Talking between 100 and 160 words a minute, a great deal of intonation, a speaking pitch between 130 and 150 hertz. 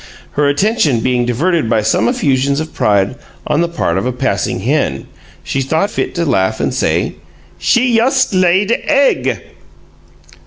Yes: average, 155 wpm; wide, 7.5 semitones; medium, 140 Hz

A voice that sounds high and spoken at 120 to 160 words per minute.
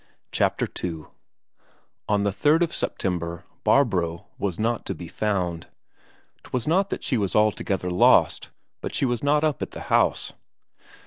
No: low, 105 Hz; average, 150 wpm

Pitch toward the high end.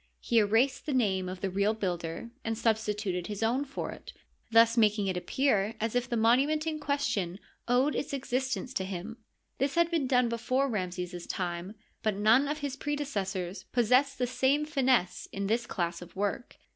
Yes: high, 230 Hz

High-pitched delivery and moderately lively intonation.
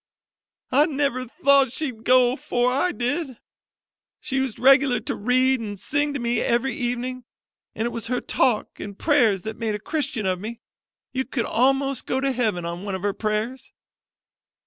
Yes: very high, 250 Hz; average, 3.4 semitones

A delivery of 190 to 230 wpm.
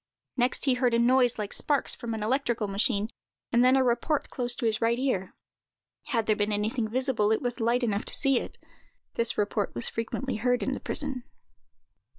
Yes: average, 195 wpm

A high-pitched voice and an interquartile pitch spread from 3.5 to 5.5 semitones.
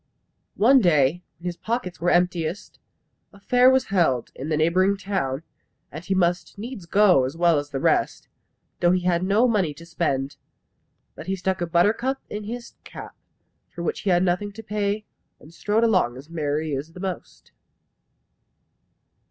No: medium, 180 Hz; average, 4.2 semitones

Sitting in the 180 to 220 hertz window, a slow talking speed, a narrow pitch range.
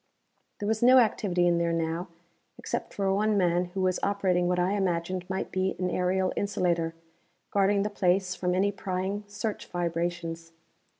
No: medium, 185 Hz; average, 165 wpm; narrow, 2.2 semitones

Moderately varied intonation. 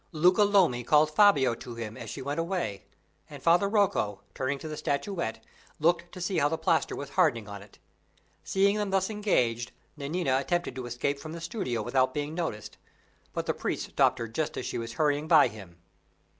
No: wide, 6.5 semitones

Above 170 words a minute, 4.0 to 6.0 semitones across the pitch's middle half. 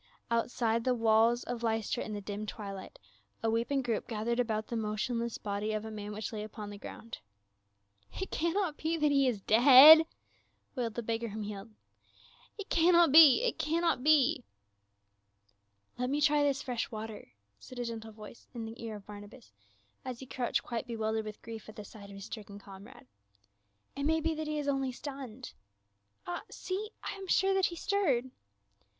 Yes: average, 200 wpm; average, 4.7 semitones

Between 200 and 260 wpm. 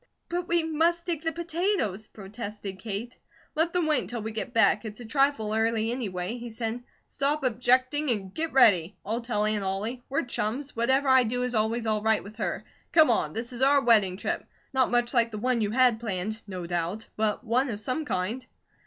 Yes: fast, 205 wpm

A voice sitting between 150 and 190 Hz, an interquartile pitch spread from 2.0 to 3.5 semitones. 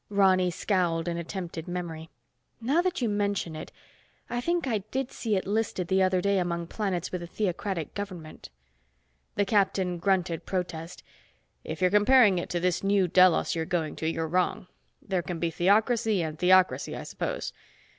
Yes: medium, 185 Hz; average, 3.0 semitones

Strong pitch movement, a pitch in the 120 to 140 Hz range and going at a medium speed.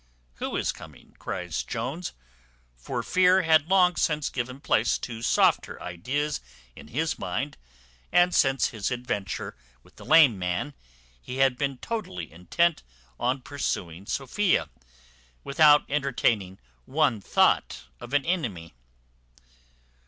No: wide, 6.4 semitones; low, 135 Hz; slow, 125 wpm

